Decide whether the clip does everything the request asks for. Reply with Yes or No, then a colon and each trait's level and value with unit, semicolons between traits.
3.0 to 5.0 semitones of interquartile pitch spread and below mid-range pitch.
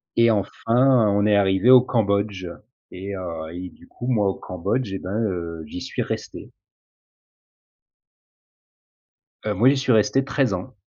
Yes: average, 4.1 semitones; low, 100 Hz